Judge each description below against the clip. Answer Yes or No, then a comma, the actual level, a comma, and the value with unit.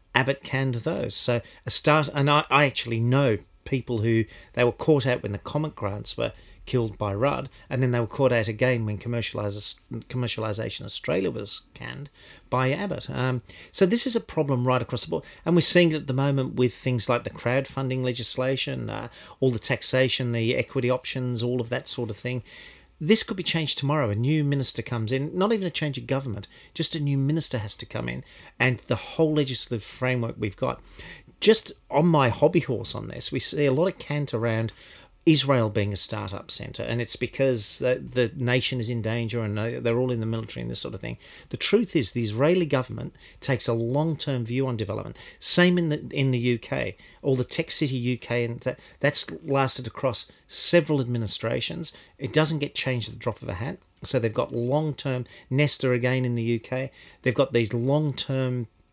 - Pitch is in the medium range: No, low, 125 Hz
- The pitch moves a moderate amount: Yes, average, 3.4 semitones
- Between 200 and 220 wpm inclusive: Yes, fast, 205 wpm